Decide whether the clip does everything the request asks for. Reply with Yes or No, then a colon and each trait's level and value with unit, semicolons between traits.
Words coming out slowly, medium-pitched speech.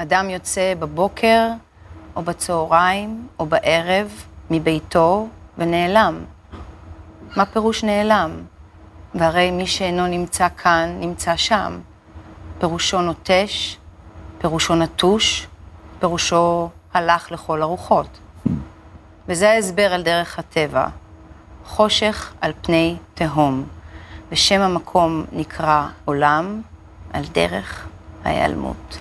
Yes: slow, 90 wpm; medium, 165 Hz